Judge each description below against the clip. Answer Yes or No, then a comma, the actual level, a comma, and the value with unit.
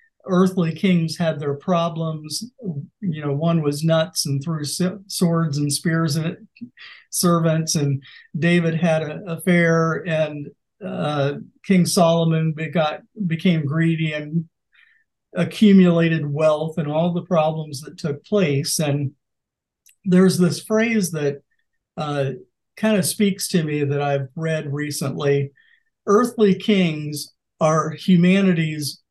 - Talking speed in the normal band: No, slow, 120 wpm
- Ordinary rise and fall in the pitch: Yes, average, 3.6 semitones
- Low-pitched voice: No, medium, 165 Hz